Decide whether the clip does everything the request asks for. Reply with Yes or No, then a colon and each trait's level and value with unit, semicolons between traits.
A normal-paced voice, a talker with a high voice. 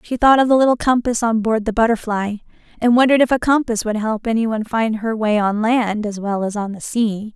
No: fast, 235 wpm; high, 225 Hz